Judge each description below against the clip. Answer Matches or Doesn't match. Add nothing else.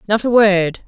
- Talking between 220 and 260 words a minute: Doesn't match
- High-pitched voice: Matches